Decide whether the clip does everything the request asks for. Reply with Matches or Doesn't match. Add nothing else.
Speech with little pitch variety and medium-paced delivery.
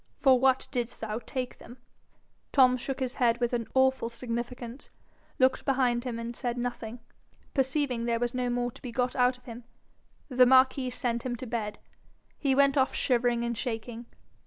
Matches